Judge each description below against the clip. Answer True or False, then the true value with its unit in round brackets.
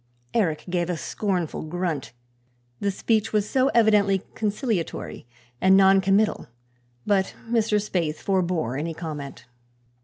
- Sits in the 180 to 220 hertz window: True (190 Hz)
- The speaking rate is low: True (115 wpm)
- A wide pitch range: False (4.1 semitones)